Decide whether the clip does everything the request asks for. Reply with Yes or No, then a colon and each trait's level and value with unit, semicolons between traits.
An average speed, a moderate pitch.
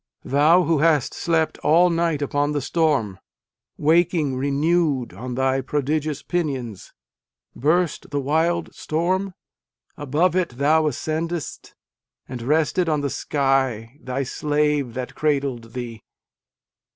No: slow, 120 wpm; medium, 145 Hz